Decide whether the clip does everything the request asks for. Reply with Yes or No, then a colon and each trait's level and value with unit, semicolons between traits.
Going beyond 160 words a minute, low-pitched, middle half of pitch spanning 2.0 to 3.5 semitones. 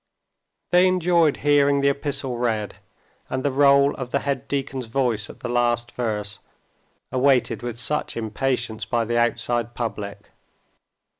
No: average, 140 wpm; low, 125 Hz; average, 2.9 semitones